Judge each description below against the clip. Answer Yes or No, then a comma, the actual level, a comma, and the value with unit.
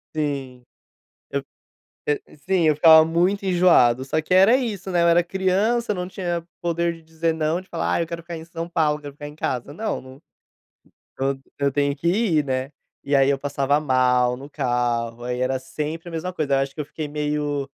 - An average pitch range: Yes, average, 3.9 semitones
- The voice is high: No, medium, 155 Hz